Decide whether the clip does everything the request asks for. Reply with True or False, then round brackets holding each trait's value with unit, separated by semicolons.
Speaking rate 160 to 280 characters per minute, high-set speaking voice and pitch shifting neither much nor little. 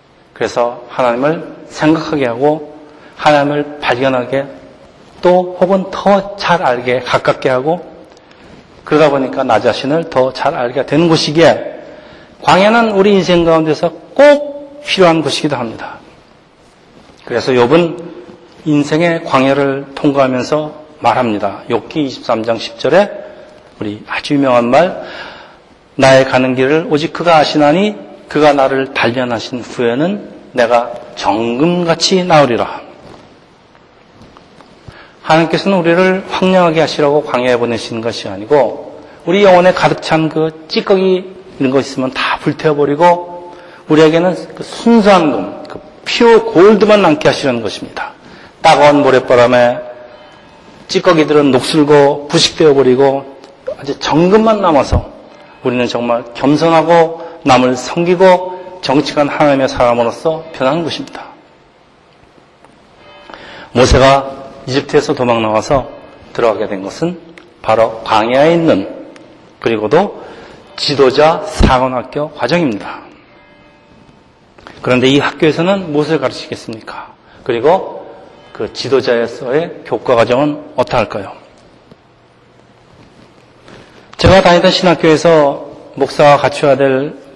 False (265 characters per minute; 150 Hz; 4.6 semitones)